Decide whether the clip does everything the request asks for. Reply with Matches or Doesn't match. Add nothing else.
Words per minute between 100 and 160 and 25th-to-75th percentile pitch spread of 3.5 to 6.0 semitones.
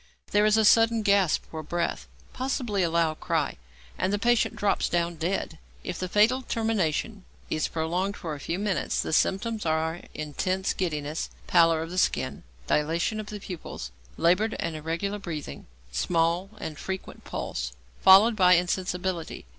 Matches